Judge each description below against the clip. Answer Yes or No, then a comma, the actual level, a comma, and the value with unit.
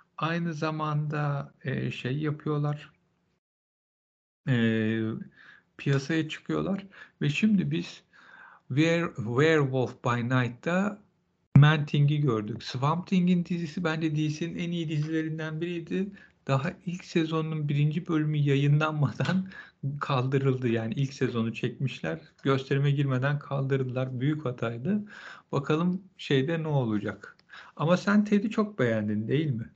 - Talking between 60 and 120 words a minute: Yes, average, 105 wpm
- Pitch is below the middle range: No, medium, 150 Hz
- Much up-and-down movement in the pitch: No, average, 4.3 semitones